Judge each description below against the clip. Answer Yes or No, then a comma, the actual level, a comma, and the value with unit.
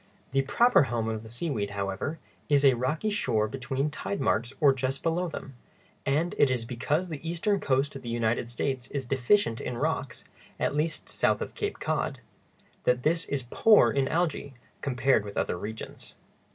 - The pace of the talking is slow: No, average, 170 wpm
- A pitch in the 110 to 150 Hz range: Yes, low, 135 Hz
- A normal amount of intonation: Yes, average, 4.5 semitones